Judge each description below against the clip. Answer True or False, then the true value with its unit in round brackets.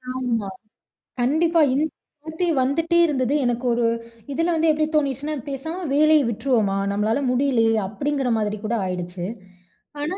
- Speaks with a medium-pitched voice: False (270 Hz)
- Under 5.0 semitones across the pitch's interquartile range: False (5.3 semitones)